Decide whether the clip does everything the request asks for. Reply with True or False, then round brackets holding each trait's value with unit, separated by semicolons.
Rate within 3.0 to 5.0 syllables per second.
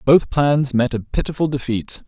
True (4.7 syllables/s)